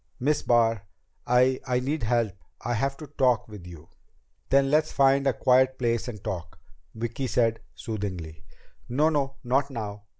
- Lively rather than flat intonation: No, average, 3.7 semitones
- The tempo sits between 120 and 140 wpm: No, average, 160 wpm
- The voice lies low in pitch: Yes, low, 125 Hz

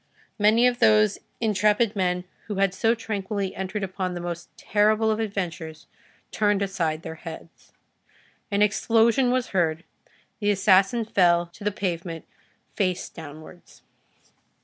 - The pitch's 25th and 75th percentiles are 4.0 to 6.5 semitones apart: No, average, 3.4 semitones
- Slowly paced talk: Yes, slow, 130 wpm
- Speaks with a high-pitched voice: Yes, high, 195 Hz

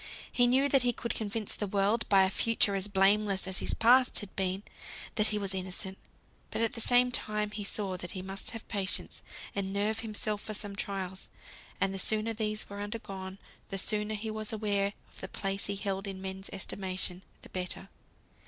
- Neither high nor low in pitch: No, high, 200 Hz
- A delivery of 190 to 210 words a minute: Yes, average, 200 wpm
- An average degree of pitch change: No, narrow, 2.1 semitones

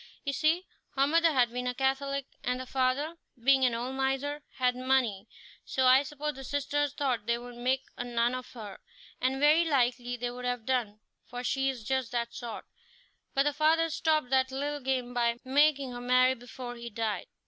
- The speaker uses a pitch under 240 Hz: No, very high, 260 Hz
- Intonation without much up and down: Yes, narrow, 2.3 semitones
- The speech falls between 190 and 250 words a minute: Yes, average, 195 wpm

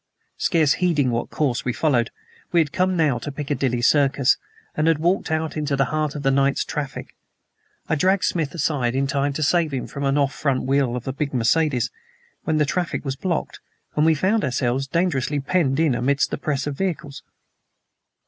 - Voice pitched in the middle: Yes, medium, 145 Hz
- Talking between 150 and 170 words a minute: No, average, 195 wpm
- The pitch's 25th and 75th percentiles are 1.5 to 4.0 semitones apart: Yes, average, 2.9 semitones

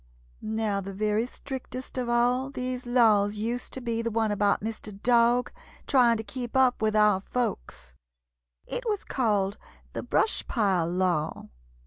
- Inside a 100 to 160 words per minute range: Yes, average, 150 wpm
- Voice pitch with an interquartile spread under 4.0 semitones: Yes, average, 3.3 semitones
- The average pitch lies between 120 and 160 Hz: No, high, 225 Hz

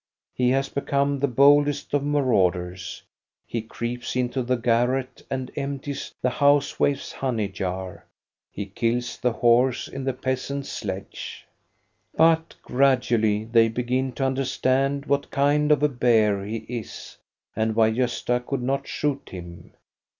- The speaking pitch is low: Yes, low, 125 Hz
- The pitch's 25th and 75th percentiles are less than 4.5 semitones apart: Yes, average, 3.4 semitones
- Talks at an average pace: Yes, average, 145 wpm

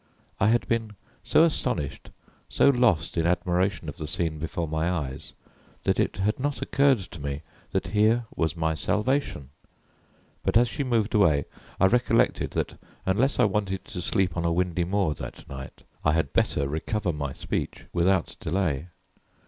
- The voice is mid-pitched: No, very low, 90 Hz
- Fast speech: No, average, 165 wpm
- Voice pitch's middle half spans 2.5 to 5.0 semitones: No, wide, 5.4 semitones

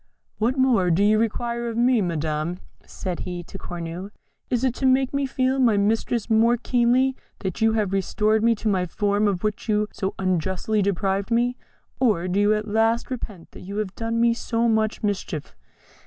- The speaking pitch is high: Yes, high, 215 Hz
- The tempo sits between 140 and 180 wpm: No, average, 190 wpm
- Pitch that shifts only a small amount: No, average, 3.6 semitones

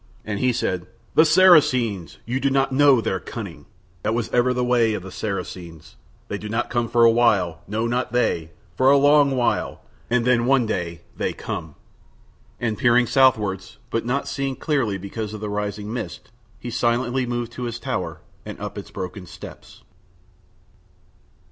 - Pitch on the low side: Yes, low, 115 Hz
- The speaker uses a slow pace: No, average, 175 wpm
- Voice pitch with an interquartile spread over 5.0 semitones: No, average, 3.7 semitones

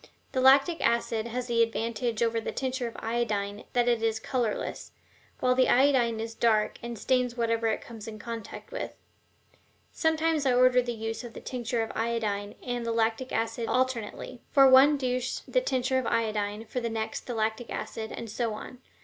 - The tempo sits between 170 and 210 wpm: Yes, average, 185 wpm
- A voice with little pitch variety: Yes, narrow, 2.1 semitones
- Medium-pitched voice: No, high, 235 Hz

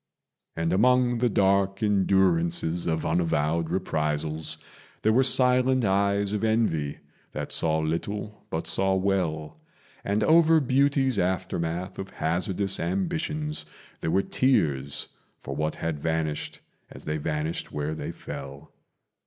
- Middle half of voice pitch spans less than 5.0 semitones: No, wide, 5.6 semitones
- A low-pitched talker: Yes, very low, 95 Hz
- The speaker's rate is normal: No, slow, 125 wpm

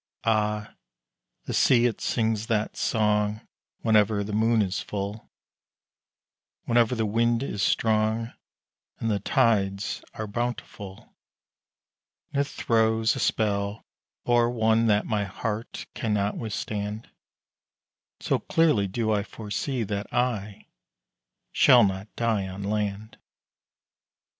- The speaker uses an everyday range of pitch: No, narrow, 1.9 semitones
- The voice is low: Yes, low, 110 Hz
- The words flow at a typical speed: No, slow, 115 wpm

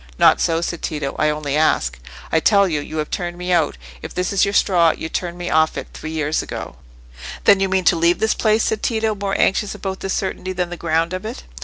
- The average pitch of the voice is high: No, medium, 175 Hz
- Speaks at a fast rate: Yes, fast, 240 wpm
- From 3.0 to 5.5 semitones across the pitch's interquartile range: Yes, average, 3.5 semitones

